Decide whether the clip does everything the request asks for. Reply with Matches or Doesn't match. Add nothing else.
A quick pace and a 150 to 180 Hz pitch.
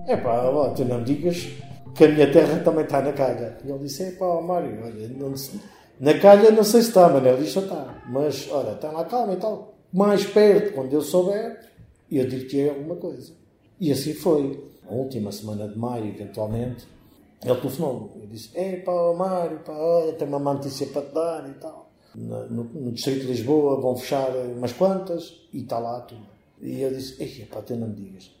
Doesn't match